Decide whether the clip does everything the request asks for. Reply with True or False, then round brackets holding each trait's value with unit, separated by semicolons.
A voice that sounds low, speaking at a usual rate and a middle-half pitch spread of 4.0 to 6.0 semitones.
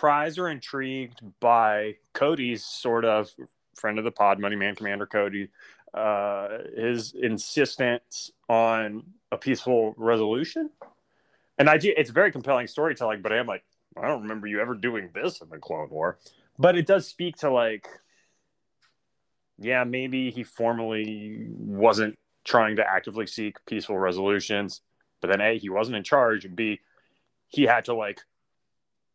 False (115 Hz; 150 wpm; 3.5 semitones)